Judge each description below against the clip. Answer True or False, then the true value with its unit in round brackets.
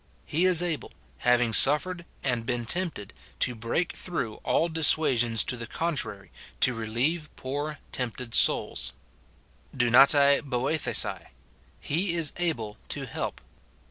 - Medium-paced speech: False (130 wpm)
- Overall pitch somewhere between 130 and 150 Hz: True (140 Hz)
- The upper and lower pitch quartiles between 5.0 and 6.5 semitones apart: True (5.3 semitones)